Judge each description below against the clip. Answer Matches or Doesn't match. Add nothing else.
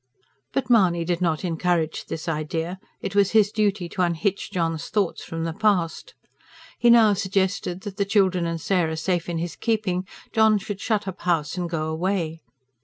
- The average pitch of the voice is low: Doesn't match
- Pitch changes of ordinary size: Matches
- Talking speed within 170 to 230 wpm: Matches